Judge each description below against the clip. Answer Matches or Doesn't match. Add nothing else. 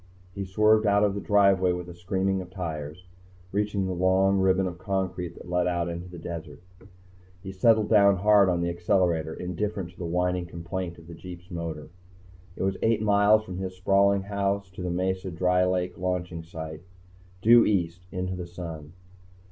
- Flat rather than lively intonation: Matches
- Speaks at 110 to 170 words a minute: Doesn't match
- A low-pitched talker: Matches